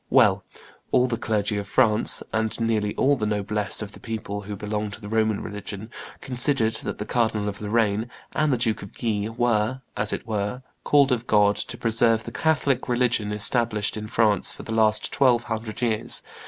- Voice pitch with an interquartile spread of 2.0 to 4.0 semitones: Yes, narrow, 2.4 semitones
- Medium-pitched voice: No, low, 110 Hz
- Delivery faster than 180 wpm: Yes, average, 190 wpm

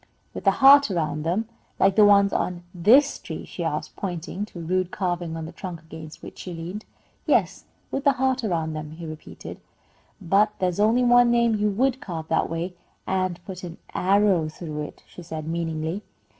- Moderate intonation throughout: Yes, average, 4.3 semitones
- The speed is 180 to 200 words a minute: Yes, average, 190 wpm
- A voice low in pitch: No, medium, 180 Hz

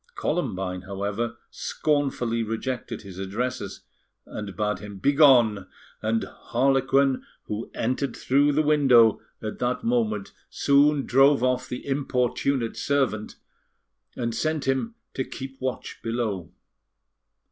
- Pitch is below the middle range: Yes, low, 125 Hz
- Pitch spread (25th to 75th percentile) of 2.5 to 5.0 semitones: Yes, average, 4.1 semitones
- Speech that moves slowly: Yes, slow, 115 wpm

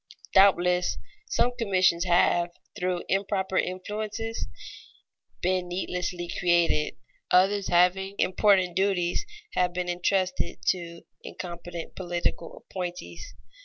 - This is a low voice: No, medium, 180 Hz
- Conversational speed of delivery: No, slow, 90 wpm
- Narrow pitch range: Yes, narrow, 1.5 semitones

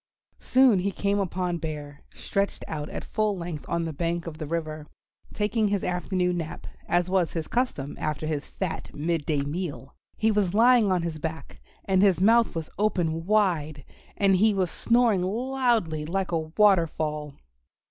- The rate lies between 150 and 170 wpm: Yes, average, 165 wpm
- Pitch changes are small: No, average, 4.4 semitones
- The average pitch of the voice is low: No, medium, 180 Hz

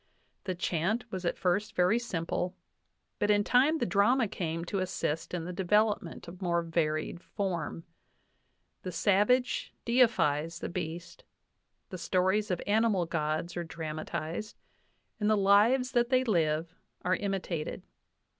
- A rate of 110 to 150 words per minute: Yes, average, 140 wpm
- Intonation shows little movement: No, average, 4.0 semitones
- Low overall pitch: No, medium, 185 Hz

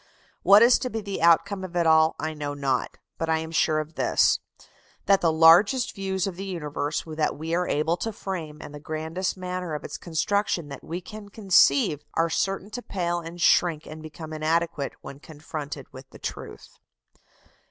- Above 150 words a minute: Yes, average, 190 wpm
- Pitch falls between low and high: Yes, medium, 165 Hz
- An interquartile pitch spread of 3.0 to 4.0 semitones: Yes, average, 3.6 semitones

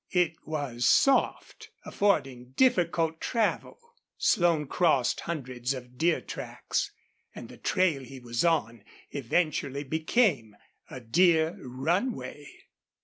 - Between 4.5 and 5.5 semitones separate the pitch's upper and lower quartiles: Yes, average, 5.2 semitones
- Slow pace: Yes, slow, 105 wpm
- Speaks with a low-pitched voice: No, medium, 155 Hz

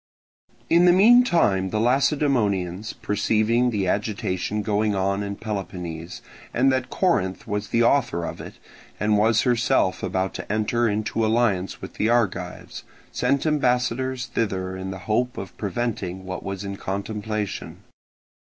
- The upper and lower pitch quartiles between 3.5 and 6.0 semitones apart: Yes, average, 4.1 semitones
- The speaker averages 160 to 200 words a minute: No, average, 140 wpm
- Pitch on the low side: Yes, low, 105 Hz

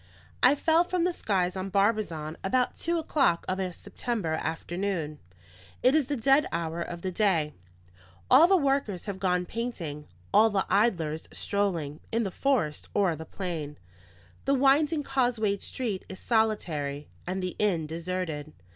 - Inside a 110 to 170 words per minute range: Yes, average, 155 wpm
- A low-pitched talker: No, high, 195 Hz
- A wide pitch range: Yes, wide, 6.9 semitones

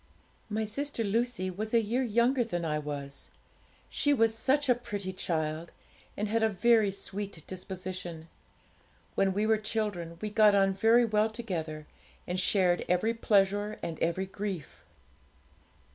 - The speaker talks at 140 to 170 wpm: Yes, average, 145 wpm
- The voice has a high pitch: Yes, high, 205 Hz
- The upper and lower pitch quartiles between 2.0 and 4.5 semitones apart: Yes, average, 3.8 semitones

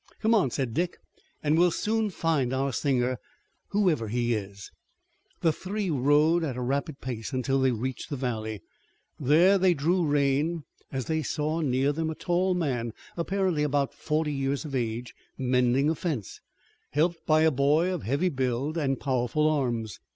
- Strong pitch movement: No, average, 4.3 semitones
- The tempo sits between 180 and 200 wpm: No, average, 165 wpm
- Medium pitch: Yes, medium, 145 Hz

